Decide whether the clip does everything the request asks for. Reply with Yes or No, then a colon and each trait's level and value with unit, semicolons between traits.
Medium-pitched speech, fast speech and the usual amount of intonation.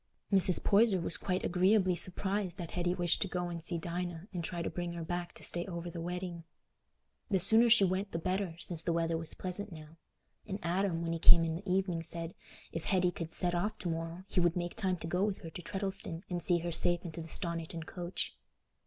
No: medium, 175 Hz; fast, 225 wpm; narrow, 1.9 semitones